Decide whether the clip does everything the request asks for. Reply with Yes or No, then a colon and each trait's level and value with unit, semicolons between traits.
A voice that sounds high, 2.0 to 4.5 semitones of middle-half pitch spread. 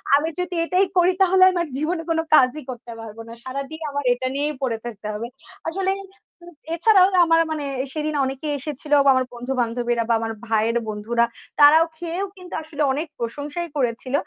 No: very high, 285 Hz; wide, 5.5 semitones